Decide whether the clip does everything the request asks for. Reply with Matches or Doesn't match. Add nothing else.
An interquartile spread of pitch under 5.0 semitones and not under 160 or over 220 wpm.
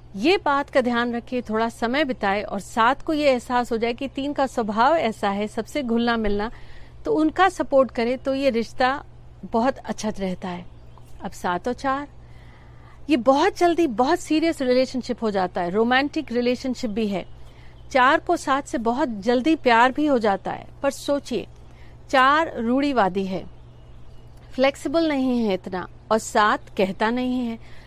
Matches